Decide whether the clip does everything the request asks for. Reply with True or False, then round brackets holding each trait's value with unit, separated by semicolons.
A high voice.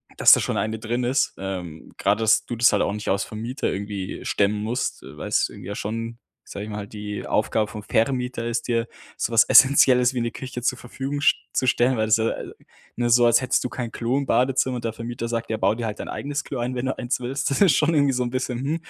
False (120 Hz)